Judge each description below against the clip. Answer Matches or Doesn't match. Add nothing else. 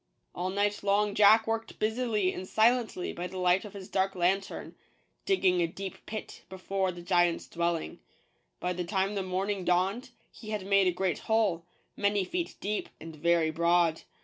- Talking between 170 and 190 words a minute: Matches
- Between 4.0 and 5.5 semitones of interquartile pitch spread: Doesn't match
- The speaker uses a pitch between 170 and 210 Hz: Matches